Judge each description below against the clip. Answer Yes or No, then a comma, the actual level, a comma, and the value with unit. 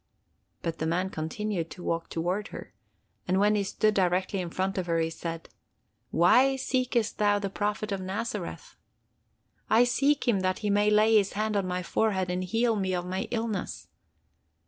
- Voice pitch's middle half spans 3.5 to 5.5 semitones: No, average, 3.0 semitones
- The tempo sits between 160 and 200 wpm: Yes, average, 175 wpm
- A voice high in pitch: Yes, high, 195 Hz